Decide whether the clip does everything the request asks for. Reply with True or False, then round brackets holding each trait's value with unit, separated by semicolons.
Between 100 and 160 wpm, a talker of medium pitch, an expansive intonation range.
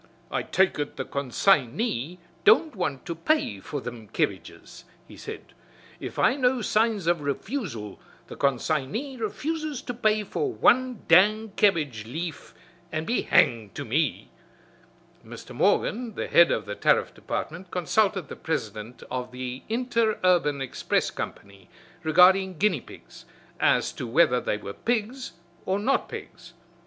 True (150 wpm; 175 Hz; 9.0 semitones)